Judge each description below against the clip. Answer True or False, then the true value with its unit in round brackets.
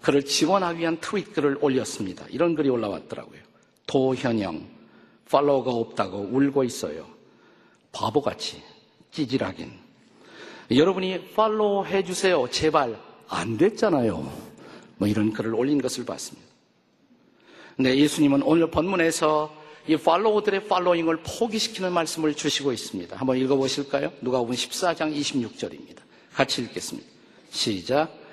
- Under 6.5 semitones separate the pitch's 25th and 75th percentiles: True (5.4 semitones)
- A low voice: False (150 Hz)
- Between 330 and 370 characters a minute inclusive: False (310 characters per minute)